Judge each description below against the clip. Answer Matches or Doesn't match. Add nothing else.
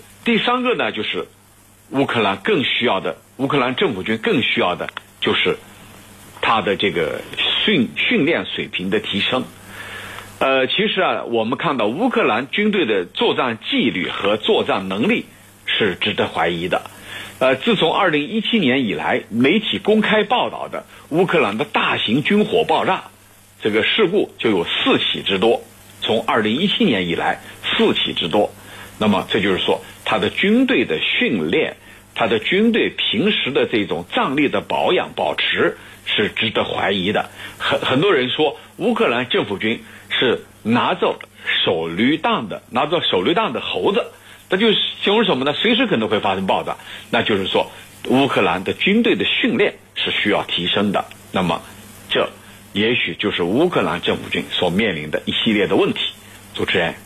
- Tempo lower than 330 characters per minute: Matches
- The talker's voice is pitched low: Doesn't match